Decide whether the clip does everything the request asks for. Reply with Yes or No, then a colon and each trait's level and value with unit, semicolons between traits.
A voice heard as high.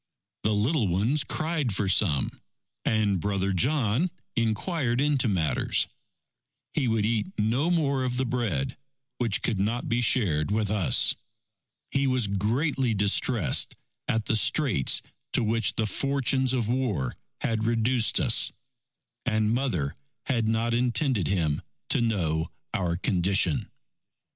No: low, 115 Hz